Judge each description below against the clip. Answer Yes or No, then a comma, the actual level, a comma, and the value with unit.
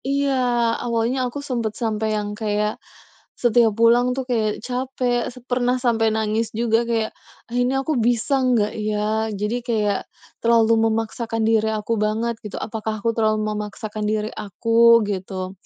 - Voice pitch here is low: No, high, 225 Hz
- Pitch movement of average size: No, narrow, 2.0 semitones